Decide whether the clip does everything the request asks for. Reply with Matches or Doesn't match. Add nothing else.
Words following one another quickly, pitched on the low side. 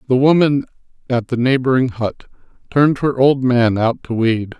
Doesn't match